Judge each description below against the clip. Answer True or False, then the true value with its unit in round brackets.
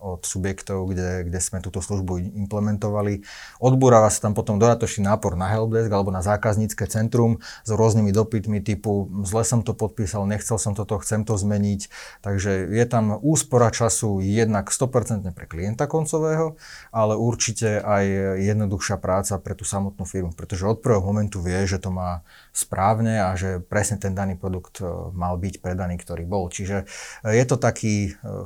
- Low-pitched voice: True (105 Hz)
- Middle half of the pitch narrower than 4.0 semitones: True (2.5 semitones)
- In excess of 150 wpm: True (160 wpm)